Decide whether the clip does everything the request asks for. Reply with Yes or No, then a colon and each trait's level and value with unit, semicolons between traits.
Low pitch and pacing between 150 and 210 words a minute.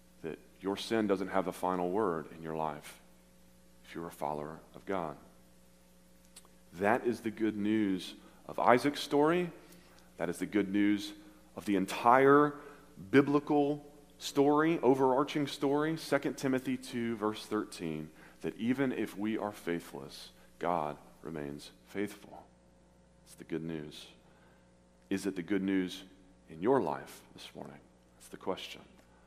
No: very low, 95 Hz; slow, 135 wpm